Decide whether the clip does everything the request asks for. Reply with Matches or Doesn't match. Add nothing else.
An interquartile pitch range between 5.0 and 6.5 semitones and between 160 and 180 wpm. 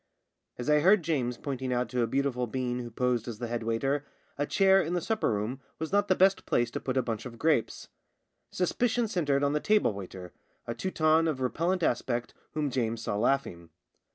Doesn't match